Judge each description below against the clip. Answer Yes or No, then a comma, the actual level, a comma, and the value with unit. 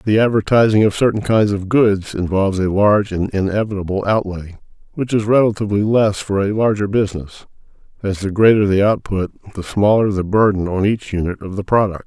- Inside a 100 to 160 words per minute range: No, average, 180 wpm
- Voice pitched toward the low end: Yes, low, 100 Hz